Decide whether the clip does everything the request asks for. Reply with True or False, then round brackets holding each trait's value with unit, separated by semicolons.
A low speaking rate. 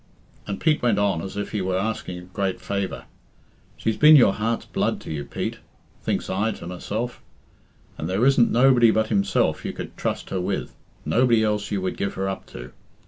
False (200 wpm)